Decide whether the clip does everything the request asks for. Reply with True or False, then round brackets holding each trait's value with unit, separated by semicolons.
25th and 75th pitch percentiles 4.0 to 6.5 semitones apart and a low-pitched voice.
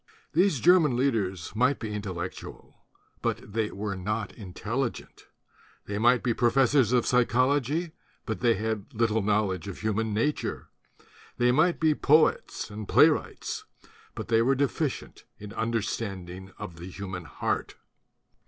True (4.3 semitones; 110 Hz)